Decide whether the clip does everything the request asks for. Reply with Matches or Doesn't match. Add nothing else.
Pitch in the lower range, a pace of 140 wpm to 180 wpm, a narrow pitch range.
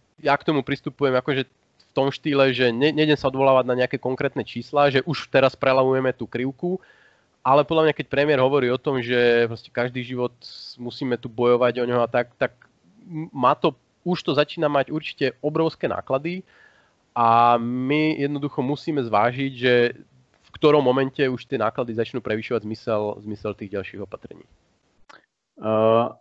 Doesn't match